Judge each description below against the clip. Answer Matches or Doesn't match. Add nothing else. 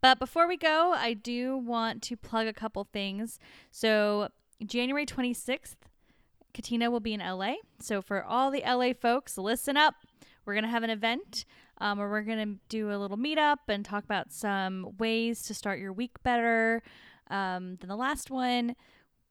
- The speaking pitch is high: Matches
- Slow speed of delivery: Doesn't match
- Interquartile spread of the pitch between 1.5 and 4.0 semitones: Matches